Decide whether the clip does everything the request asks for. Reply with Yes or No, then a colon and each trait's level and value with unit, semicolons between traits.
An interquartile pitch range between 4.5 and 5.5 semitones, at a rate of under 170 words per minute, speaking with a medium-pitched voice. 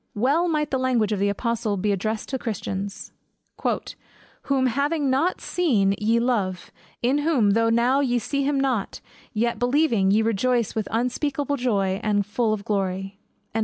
No: average, 4.8 semitones; average, 160 wpm; high, 235 Hz